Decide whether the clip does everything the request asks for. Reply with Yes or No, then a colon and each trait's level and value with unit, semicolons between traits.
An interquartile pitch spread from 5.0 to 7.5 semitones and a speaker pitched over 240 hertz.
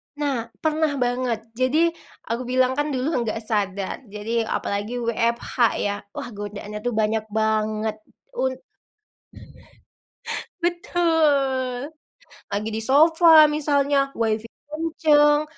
Yes: average, 5.3 semitones; very high, 250 Hz